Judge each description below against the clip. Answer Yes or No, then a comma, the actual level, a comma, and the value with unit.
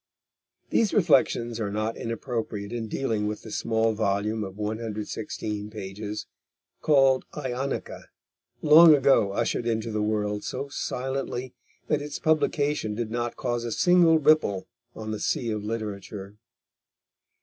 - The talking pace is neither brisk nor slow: No, slow, 130 wpm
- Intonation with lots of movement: No, average, 4.2 semitones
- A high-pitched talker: No, low, 115 Hz